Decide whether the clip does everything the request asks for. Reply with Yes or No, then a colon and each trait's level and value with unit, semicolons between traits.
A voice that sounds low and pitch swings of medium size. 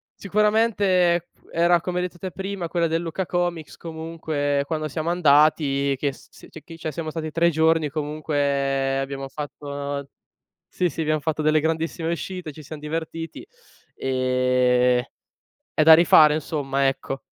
No: medium, 155 Hz; average, 3.1 semitones